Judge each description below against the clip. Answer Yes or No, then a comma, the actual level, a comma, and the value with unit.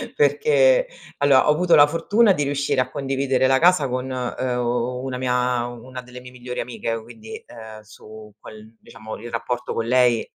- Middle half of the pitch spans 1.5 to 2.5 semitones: No, average, 2.9 semitones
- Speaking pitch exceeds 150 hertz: No, low, 125 Hz